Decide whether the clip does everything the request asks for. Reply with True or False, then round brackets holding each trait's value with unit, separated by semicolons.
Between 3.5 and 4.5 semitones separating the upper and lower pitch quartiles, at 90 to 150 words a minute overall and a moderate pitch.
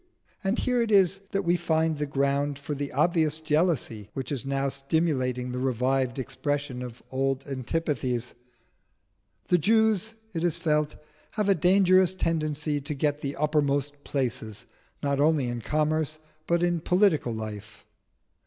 True (3.8 semitones; 145 wpm; 145 Hz)